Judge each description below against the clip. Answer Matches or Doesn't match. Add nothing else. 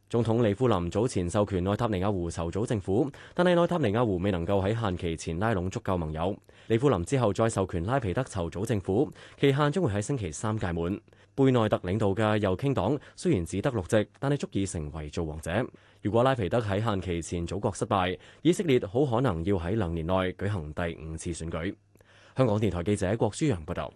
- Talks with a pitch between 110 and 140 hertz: Doesn't match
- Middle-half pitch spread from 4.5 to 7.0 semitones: Matches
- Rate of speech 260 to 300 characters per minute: Doesn't match